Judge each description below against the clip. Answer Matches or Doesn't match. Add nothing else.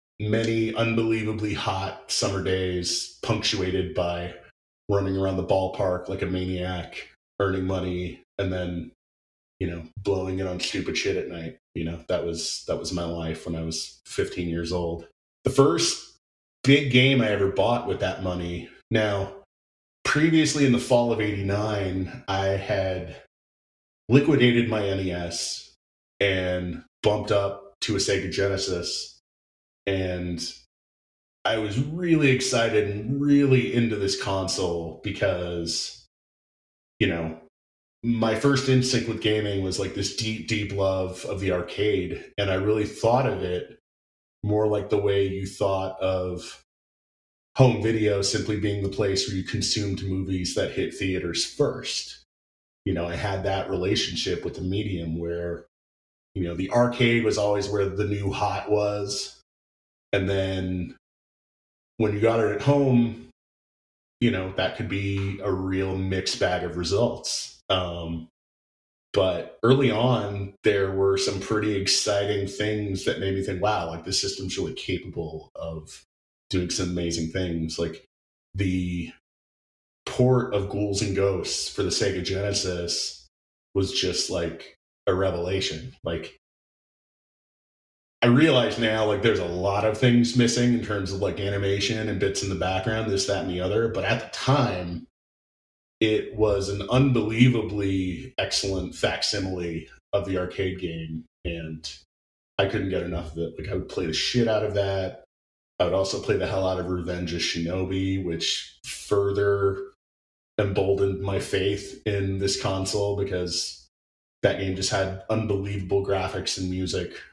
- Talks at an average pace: Matches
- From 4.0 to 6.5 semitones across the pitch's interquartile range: Doesn't match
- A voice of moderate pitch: Doesn't match